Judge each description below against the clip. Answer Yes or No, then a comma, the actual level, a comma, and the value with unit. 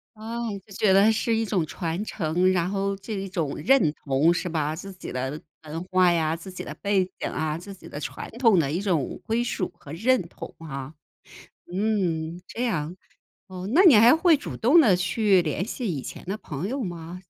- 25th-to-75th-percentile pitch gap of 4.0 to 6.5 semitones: Yes, average, 5.0 semitones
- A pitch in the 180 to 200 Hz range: Yes, medium, 185 Hz